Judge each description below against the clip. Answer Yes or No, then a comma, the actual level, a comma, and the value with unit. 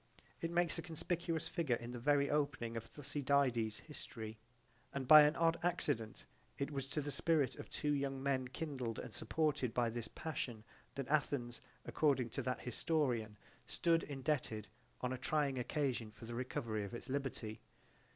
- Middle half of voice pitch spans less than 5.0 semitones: Yes, average, 4.1 semitones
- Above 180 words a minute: No, average, 165 wpm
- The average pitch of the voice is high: No, low, 135 Hz